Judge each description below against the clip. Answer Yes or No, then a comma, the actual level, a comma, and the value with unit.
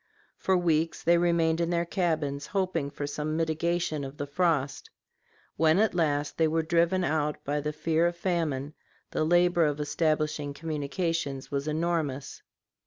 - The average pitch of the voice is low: No, medium, 160 Hz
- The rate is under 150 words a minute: No, average, 155 wpm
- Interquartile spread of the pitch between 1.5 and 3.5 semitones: Yes, narrow, 2.6 semitones